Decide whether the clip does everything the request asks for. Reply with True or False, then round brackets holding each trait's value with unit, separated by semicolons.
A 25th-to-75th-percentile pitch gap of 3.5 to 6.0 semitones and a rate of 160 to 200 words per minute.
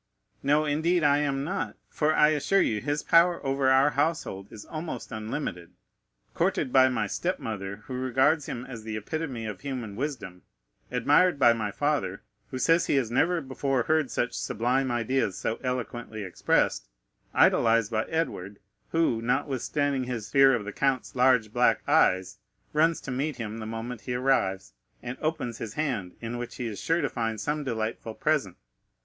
True (4.7 semitones; 170 wpm)